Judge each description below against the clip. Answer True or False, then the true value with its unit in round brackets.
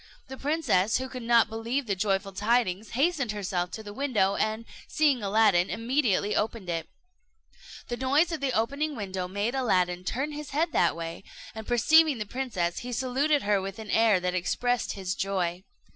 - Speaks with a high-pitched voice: True (220 Hz)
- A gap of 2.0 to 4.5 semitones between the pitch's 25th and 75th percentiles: False (5.3 semitones)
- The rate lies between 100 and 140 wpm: False (175 wpm)